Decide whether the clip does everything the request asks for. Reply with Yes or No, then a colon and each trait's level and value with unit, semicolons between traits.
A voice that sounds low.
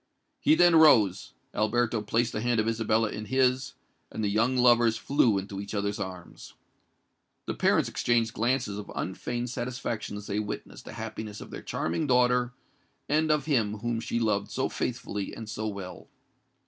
Yes: low, 115 Hz